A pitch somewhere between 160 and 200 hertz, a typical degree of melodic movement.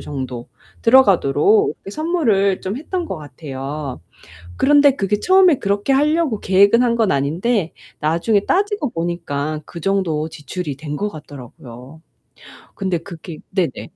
No: high, 190 Hz; wide, 8.2 semitones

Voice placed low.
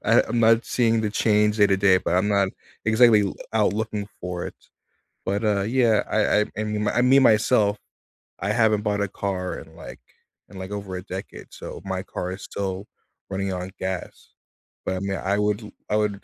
Yes: low, 105 Hz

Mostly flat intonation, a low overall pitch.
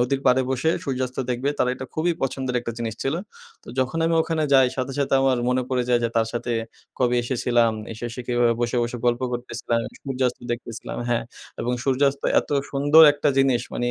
Yes: narrow, 2.0 semitones; low, 125 Hz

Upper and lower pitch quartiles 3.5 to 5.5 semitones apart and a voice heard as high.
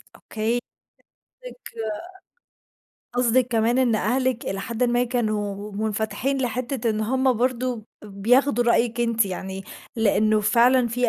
No: narrow, 2.6 semitones; high, 235 Hz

